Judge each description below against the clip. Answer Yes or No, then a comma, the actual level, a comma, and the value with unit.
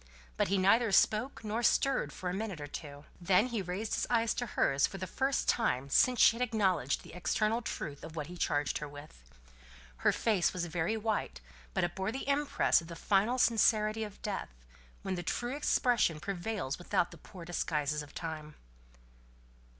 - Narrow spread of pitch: No, wide, 5.6 semitones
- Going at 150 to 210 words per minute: Yes, average, 190 wpm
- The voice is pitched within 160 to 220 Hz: Yes, high, 190 Hz